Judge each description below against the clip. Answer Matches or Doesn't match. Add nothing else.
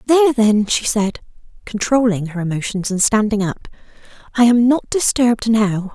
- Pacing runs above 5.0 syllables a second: Doesn't match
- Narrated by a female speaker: Matches